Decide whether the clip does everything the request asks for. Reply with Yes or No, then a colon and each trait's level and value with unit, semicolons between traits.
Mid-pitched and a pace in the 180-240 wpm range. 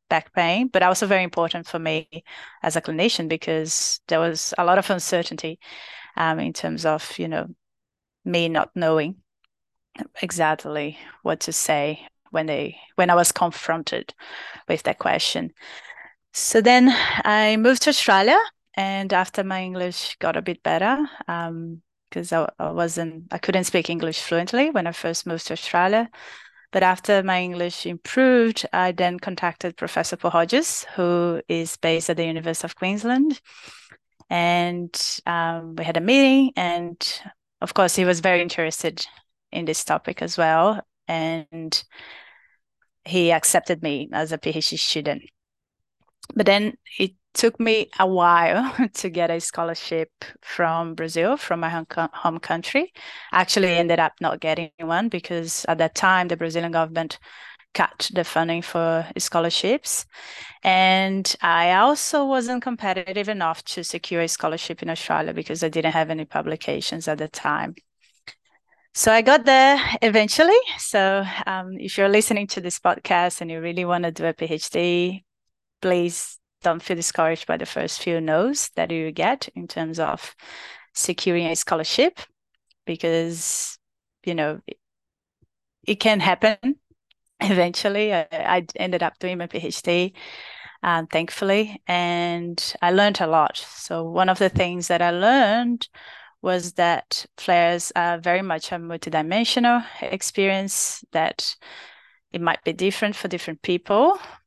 No: medium, 175 Hz; average, 150 wpm